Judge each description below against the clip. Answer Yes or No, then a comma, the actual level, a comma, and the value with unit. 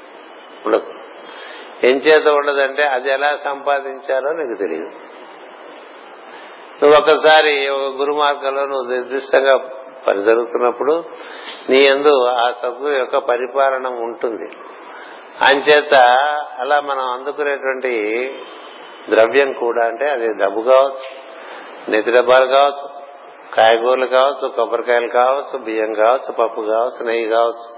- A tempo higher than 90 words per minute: Yes, average, 100 wpm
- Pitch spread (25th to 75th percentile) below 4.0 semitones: Yes, narrow, 2.6 semitones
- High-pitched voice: No, low, 135 Hz